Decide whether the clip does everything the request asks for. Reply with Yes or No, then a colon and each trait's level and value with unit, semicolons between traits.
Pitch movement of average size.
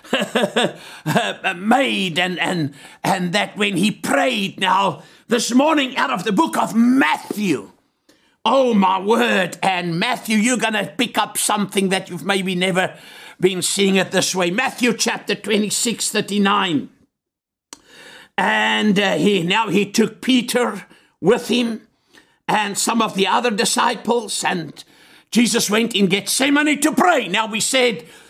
Yes: average, 4.0 semitones